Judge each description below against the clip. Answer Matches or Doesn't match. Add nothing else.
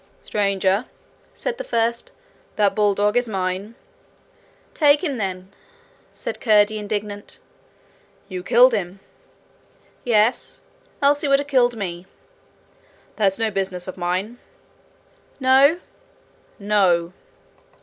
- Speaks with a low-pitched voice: Doesn't match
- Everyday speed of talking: Doesn't match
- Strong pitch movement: Doesn't match